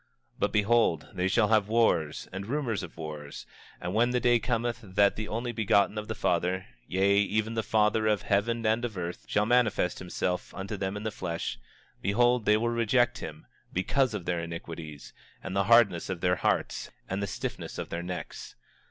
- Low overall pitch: Yes, low, 105 Hz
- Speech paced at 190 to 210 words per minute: Yes, average, 195 wpm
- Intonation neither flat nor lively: Yes, average, 4.1 semitones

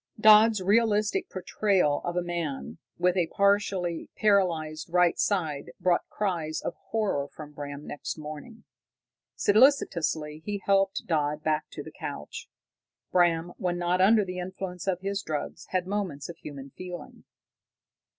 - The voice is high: No, medium, 180 Hz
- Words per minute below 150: Yes, average, 140 wpm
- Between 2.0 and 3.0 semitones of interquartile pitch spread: No, average, 4.3 semitones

